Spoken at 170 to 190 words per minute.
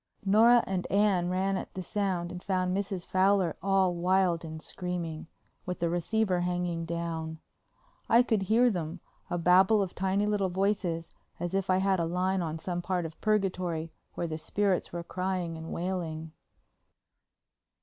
No: average, 160 wpm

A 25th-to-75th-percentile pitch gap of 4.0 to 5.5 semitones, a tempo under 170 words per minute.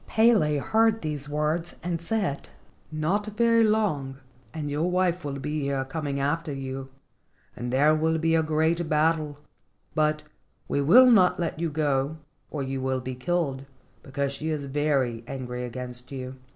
No: average, 3.6 semitones; average, 160 wpm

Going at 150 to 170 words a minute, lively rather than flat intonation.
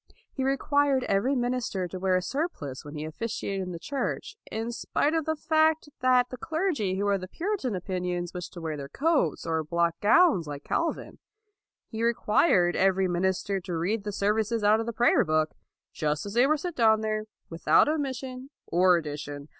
No: average, 195 wpm; wide, 6.9 semitones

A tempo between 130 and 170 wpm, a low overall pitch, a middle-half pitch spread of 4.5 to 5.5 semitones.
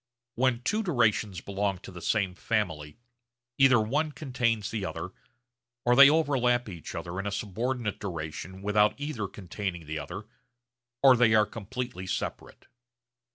Yes: average, 145 wpm; low, 105 Hz; average, 4.8 semitones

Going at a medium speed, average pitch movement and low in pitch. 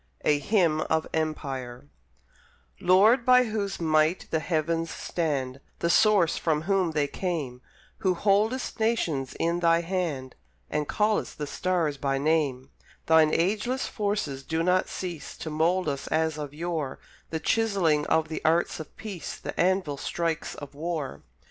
No: average, 150 wpm; average, 3.8 semitones; medium, 165 Hz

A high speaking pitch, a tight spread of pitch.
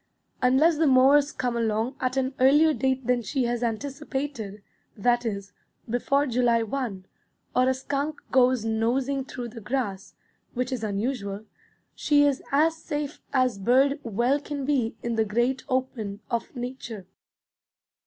No: very high, 255 Hz; average, 3.4 semitones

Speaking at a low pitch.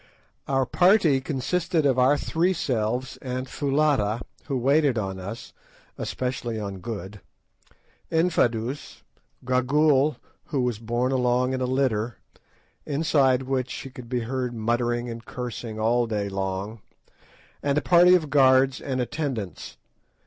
Yes: low, 130 Hz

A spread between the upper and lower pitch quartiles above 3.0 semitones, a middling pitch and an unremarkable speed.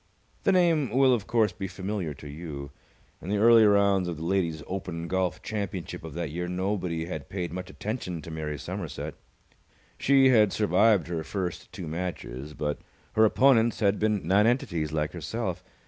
No: average, 4.5 semitones; very low, 95 Hz; average, 170 wpm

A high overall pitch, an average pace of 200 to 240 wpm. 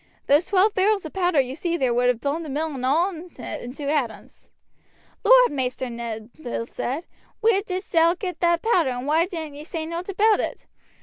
Yes: very high, 320 Hz; fast, 205 wpm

